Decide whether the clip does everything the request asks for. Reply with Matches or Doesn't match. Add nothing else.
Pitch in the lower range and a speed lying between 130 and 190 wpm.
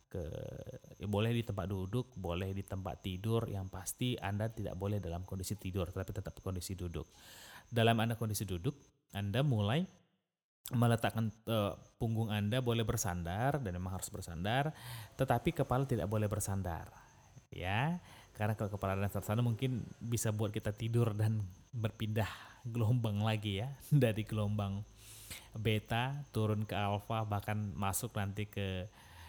Matches